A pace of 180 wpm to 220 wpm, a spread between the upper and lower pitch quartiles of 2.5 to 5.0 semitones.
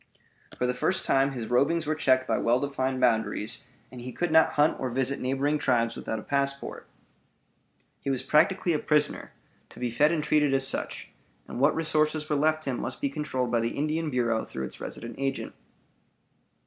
Yes: average, 190 wpm; average, 3.4 semitones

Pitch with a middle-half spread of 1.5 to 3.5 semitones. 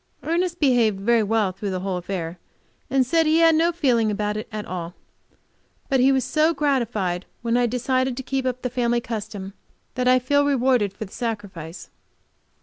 No: average, 4.6 semitones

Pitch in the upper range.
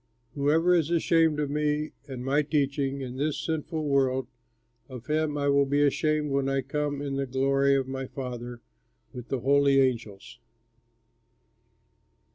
No: medium, 140 Hz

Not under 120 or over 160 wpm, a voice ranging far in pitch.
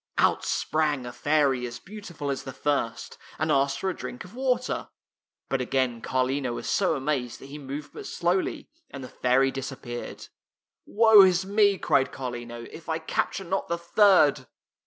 No: average, 180 wpm; wide, 5.9 semitones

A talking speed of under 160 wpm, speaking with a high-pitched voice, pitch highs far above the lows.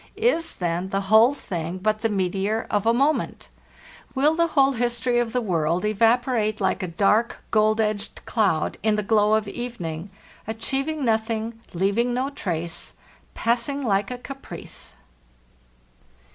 No: average, 145 wpm; high, 220 Hz; average, 3.9 semitones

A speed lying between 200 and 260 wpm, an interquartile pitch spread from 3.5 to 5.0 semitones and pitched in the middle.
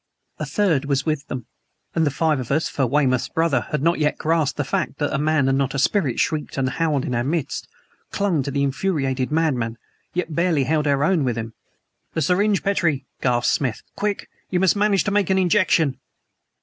Yes: fast, 205 wpm; average, 4.1 semitones; medium, 150 Hz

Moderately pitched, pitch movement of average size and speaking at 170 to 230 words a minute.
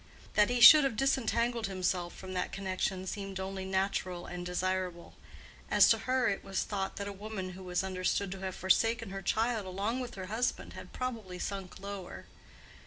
No: high, 195 Hz; average, 3.1 semitones; average, 180 wpm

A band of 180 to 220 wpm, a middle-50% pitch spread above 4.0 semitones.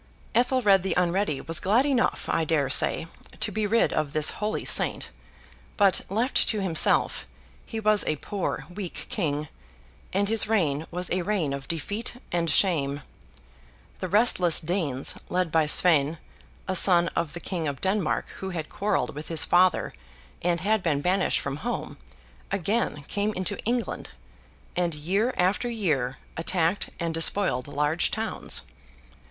No: average, 150 wpm; average, 4.7 semitones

